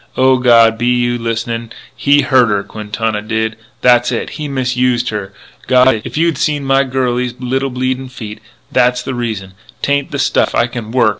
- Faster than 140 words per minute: Yes, average, 180 wpm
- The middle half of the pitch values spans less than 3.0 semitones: Yes, narrow, 2.4 semitones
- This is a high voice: No, low, 125 Hz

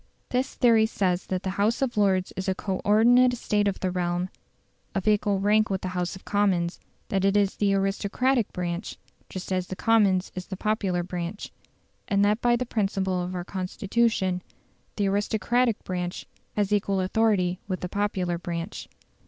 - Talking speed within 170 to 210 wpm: Yes, average, 175 wpm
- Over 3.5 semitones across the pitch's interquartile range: No, narrow, 2.4 semitones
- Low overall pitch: No, high, 195 Hz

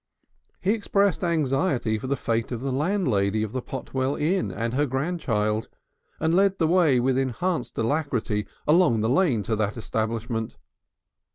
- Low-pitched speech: Yes, low, 130 Hz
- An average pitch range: No, wide, 6.7 semitones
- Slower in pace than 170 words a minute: Yes, average, 155 wpm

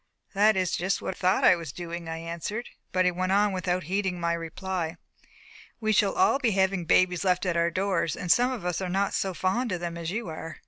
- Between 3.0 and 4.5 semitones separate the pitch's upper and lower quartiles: No, narrow, 2.5 semitones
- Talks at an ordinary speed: No, fast, 235 wpm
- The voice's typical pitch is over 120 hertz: Yes, medium, 185 Hz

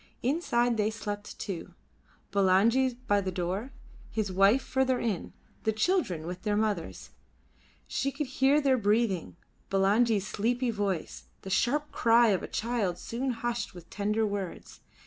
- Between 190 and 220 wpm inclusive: No, average, 145 wpm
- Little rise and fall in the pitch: No, average, 3.8 semitones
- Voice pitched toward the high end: Yes, high, 220 Hz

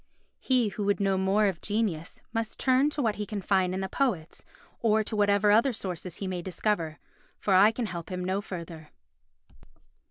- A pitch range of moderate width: Yes, average, 3.0 semitones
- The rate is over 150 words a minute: Yes, average, 190 wpm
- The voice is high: Yes, high, 200 Hz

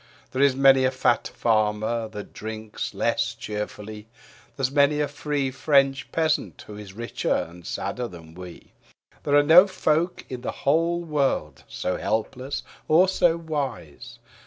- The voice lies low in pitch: Yes, low, 130 Hz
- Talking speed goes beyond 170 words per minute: No, average, 155 wpm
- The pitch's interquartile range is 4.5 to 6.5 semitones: Yes, wide, 5.5 semitones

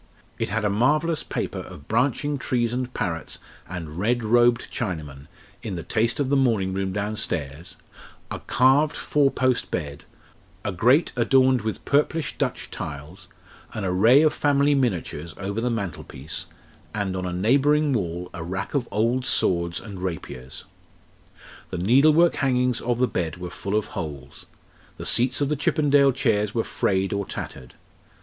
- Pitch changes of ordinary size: No, wide, 6.3 semitones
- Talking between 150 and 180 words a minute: Yes, average, 155 wpm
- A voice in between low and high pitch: No, low, 110 Hz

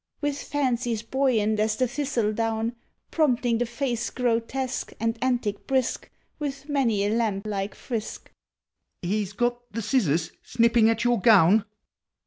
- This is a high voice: Yes, high, 230 Hz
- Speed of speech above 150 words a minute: No, average, 140 wpm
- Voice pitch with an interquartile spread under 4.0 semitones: Yes, average, 3.0 semitones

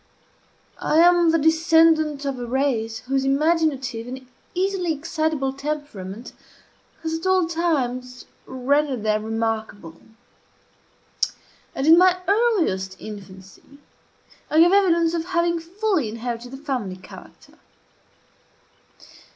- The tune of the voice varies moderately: No, wide, 5.7 semitones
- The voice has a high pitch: Yes, very high, 285 Hz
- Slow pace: Yes, slow, 110 wpm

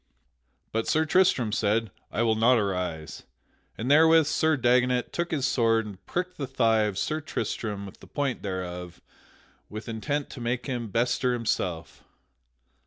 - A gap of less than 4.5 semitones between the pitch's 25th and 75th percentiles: No, average, 4.8 semitones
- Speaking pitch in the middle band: No, low, 115 Hz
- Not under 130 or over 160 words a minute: Yes, average, 155 wpm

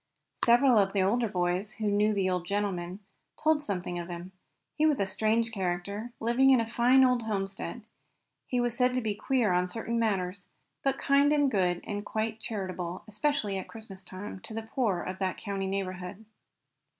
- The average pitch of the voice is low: No, high, 210 Hz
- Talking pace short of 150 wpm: No, average, 185 wpm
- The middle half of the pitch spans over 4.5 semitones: No, average, 4.0 semitones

